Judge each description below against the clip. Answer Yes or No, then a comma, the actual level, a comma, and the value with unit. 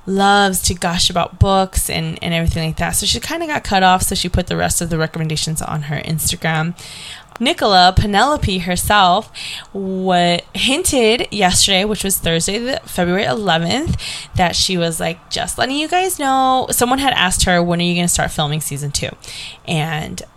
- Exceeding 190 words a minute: No, average, 185 wpm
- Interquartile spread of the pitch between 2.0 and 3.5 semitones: No, average, 4.0 semitones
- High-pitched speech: No, medium, 180 Hz